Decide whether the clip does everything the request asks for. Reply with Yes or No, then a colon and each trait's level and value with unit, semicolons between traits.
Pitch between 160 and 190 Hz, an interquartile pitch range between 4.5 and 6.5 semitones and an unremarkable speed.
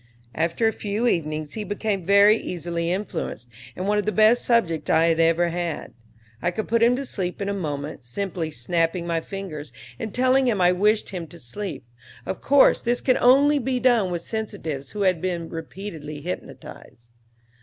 Yes: medium, 185 Hz; average, 4.8 semitones; average, 185 wpm